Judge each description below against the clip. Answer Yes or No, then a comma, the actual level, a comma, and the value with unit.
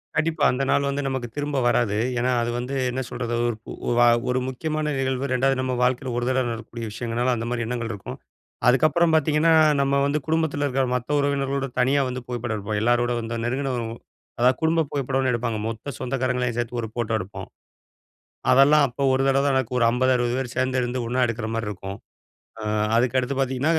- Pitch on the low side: Yes, low, 130 Hz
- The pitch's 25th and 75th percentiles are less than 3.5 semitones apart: Yes, narrow, 2.4 semitones